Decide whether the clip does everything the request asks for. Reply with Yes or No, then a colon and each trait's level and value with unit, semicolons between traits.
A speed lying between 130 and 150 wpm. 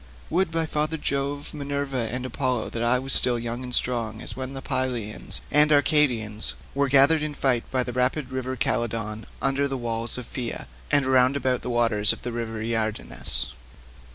No: average, 180 wpm